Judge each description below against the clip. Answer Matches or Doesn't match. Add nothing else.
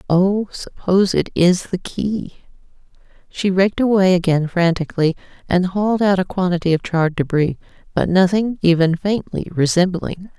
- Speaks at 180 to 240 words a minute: Doesn't match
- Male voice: Doesn't match